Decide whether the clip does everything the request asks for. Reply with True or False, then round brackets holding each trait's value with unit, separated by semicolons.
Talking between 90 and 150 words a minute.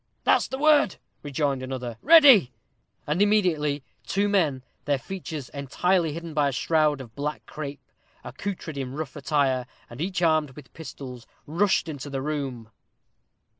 True (145 wpm)